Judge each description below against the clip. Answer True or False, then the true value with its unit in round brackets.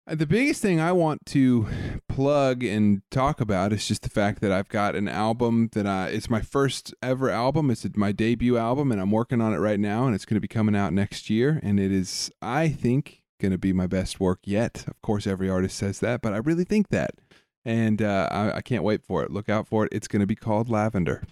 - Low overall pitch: True (110 Hz)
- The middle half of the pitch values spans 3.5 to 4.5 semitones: True (3.9 semitones)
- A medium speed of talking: False (240 wpm)